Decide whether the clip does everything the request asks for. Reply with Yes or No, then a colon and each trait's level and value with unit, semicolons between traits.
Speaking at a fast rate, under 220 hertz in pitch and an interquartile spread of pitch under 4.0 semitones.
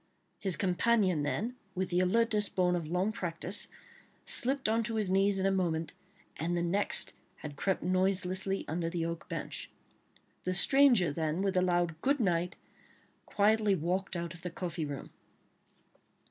No: average, 160 wpm; medium, 185 Hz; average, 2.9 semitones